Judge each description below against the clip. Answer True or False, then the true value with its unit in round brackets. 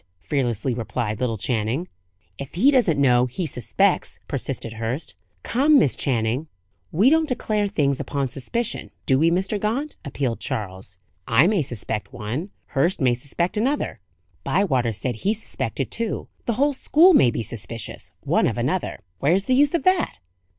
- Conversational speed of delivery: True (155 wpm)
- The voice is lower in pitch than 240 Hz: True (140 Hz)